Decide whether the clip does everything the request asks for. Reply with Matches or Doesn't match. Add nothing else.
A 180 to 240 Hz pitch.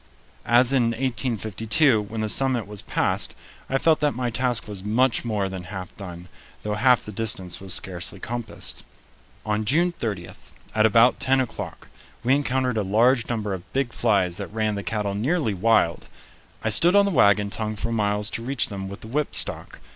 Doesn't match